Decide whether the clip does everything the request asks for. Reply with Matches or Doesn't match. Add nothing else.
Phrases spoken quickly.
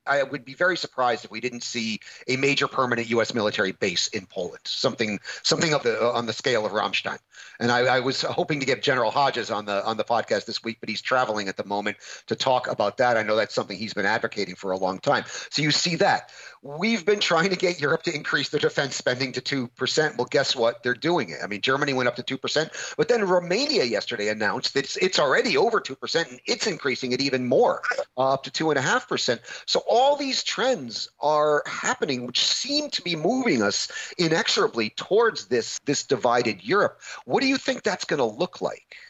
Matches